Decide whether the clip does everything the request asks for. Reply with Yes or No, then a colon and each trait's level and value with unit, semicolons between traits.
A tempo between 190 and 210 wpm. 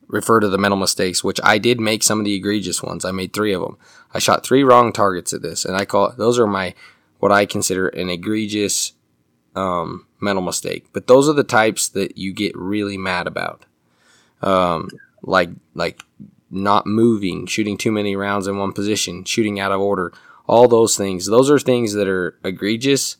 Yes: average, 200 wpm